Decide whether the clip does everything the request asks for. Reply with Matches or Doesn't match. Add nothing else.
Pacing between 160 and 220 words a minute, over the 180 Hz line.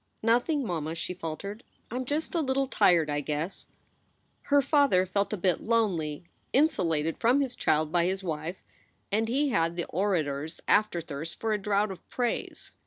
Matches